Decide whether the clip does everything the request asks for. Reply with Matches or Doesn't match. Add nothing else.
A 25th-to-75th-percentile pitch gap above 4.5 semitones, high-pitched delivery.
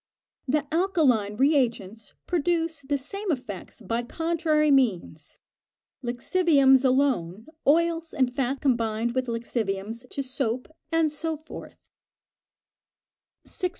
Matches